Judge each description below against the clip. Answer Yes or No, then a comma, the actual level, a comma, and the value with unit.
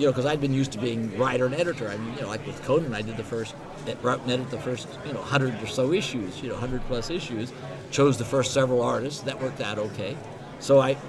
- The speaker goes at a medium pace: No, fast, 265 wpm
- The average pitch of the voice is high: No, low, 130 Hz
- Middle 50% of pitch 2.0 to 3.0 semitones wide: Yes, narrow, 2.6 semitones